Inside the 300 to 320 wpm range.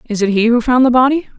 Yes: fast, 305 wpm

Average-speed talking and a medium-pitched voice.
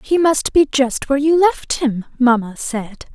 No: average, 190 wpm; very high, 270 Hz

